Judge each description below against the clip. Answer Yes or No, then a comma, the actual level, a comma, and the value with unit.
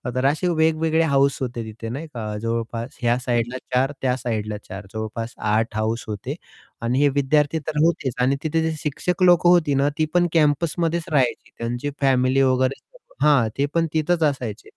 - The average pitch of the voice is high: No, low, 135 Hz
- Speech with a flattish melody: No, average, 5.0 semitones